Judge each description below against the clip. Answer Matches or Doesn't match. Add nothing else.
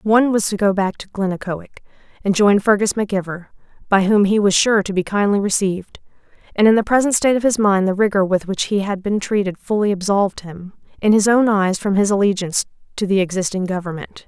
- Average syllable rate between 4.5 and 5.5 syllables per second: Doesn't match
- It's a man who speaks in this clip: Doesn't match